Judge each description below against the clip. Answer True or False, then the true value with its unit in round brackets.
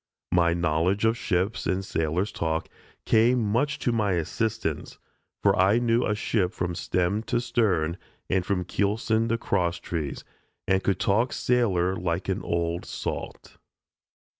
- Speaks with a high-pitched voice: False (95 Hz)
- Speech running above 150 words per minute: False (145 wpm)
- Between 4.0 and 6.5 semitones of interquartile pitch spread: True (4.4 semitones)